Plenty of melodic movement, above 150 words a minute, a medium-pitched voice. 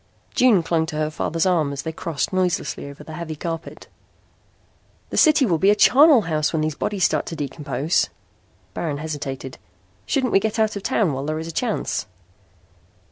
No: average, 4.7 semitones; average, 185 wpm; medium, 165 Hz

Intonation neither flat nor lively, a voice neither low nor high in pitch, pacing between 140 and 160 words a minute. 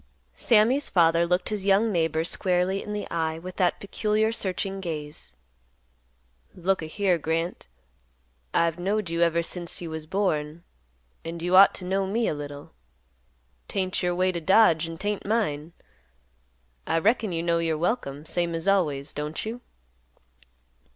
Yes: average, 3.3 semitones; medium, 175 Hz; average, 155 wpm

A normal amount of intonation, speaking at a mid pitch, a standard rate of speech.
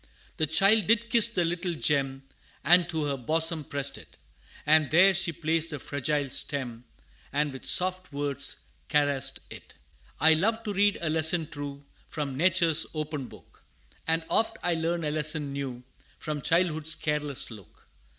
Yes: average, 3.3 semitones; medium, 155 Hz; average, 160 wpm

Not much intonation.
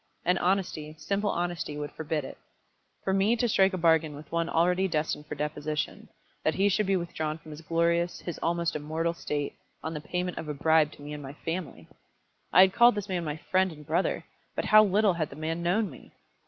No: average, 3.5 semitones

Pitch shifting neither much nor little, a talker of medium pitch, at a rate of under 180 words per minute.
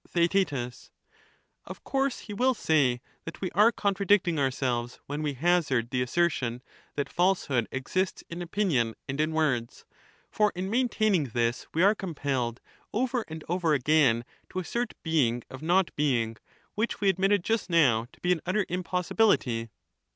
No: wide, 7.0 semitones; medium, 165 Hz; average, 150 wpm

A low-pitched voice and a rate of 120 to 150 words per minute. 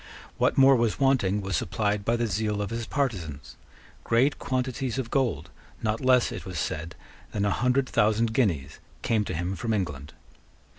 No: low, 110 Hz; average, 170 wpm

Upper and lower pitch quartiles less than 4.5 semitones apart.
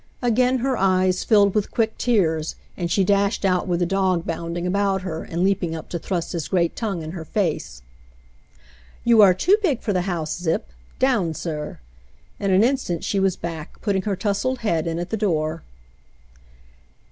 Yes: average, 3.6 semitones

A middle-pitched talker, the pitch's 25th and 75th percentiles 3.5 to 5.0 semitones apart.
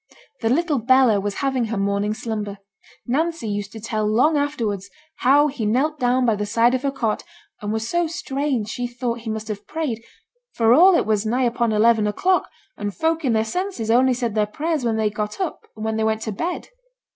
No: high, 230 Hz; average, 4.2 semitones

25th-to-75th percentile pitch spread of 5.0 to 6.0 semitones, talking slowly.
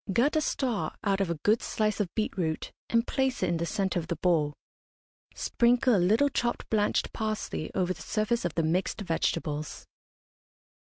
No: wide, 5.4 semitones; average, 180 wpm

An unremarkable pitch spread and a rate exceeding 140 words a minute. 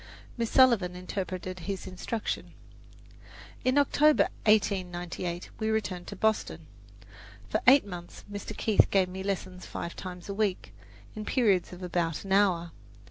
No: average, 3.2 semitones; slow, 135 wpm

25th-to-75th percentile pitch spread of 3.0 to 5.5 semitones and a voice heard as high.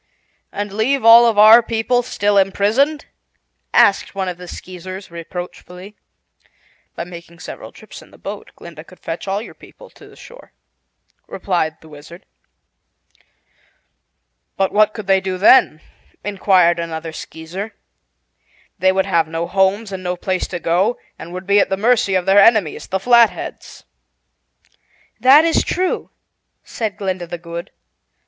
Yes: average, 3.4 semitones; high, 195 Hz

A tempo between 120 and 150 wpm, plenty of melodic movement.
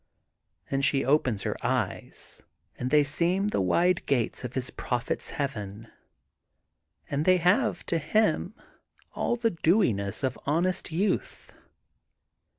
Yes: average, 140 wpm; wide, 6.3 semitones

